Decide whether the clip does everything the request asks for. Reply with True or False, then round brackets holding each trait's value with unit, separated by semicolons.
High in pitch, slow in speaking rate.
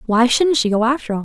False (245 Hz; 290 wpm)